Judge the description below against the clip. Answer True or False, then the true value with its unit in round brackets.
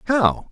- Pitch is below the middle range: False (190 Hz)